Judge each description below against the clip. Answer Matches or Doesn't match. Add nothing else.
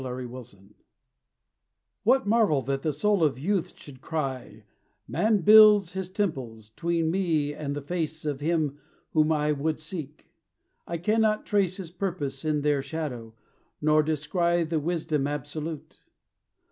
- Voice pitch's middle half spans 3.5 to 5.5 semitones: Matches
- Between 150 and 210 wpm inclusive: Doesn't match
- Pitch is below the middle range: Doesn't match